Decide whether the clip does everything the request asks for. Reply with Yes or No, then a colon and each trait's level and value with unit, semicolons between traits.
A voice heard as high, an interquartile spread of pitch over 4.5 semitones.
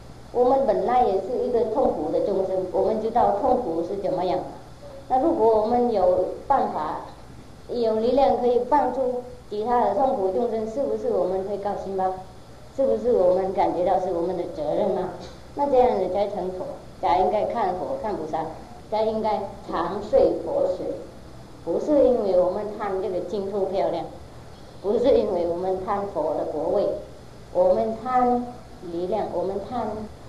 Yes: high, 215 Hz; average, 5.2 semitones